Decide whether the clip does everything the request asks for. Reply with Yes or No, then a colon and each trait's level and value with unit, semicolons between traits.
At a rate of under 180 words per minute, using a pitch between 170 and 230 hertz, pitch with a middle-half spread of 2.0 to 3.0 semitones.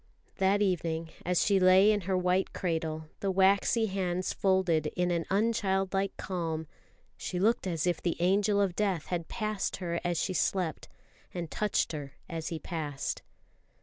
Yes: average, 160 wpm; medium, 185 Hz; average, 2.7 semitones